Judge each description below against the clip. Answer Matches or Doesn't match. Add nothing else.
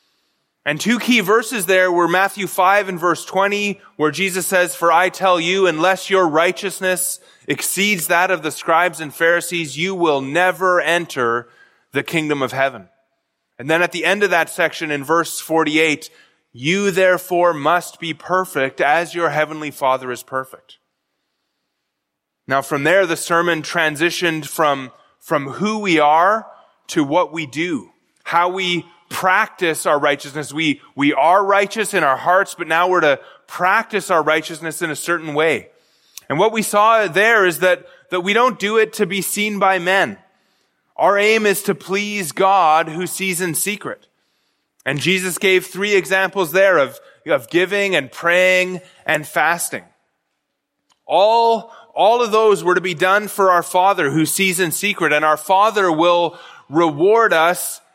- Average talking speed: Matches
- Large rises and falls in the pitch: Doesn't match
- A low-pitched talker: Doesn't match